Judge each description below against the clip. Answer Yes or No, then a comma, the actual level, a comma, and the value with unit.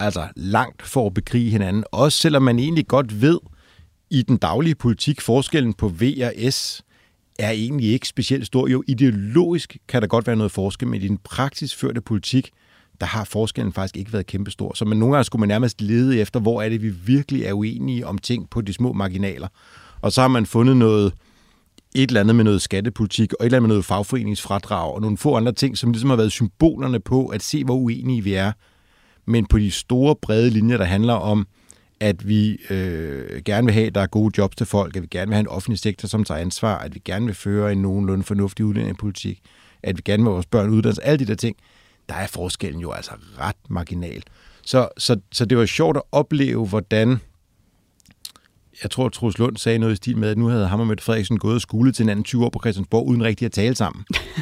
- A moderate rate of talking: No, fast, 230 wpm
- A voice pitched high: No, low, 110 Hz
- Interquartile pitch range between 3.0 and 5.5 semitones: Yes, average, 3.5 semitones